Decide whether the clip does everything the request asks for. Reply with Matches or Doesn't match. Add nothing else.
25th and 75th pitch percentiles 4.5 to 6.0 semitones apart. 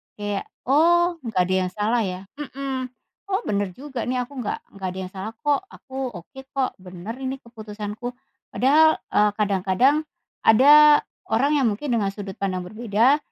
Matches